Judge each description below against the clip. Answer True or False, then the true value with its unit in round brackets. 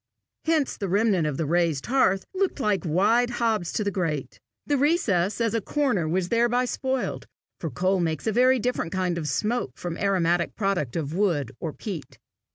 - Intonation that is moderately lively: False (6.0 semitones)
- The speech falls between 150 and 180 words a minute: False (190 wpm)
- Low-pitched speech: False (195 Hz)